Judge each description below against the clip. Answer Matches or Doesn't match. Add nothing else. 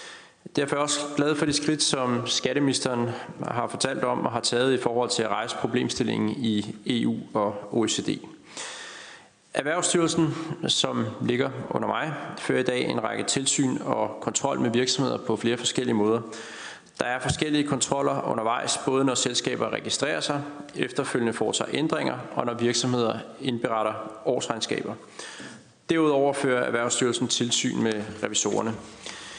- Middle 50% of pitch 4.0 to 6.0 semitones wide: Doesn't match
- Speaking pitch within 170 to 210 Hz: Doesn't match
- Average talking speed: Doesn't match